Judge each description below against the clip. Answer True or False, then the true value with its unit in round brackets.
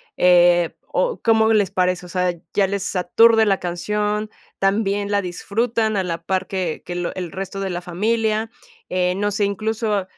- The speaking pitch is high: True (195 Hz)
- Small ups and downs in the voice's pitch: False (3.0 semitones)